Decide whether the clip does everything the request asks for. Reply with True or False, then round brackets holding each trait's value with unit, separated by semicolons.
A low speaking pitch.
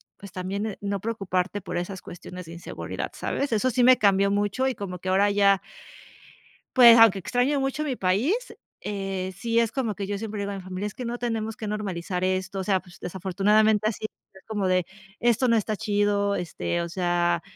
False (200 Hz)